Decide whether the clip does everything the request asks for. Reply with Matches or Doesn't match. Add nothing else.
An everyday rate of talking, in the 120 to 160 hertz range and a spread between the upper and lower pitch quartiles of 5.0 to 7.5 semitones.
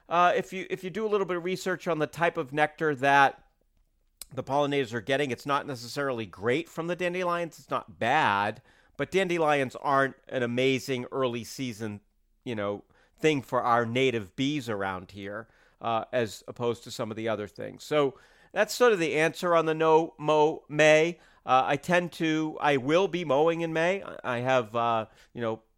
Matches